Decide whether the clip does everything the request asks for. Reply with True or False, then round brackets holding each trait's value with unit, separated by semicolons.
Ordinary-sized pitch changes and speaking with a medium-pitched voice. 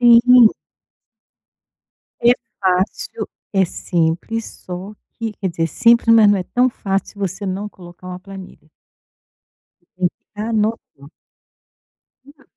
False (3.9 semitones; 195 Hz)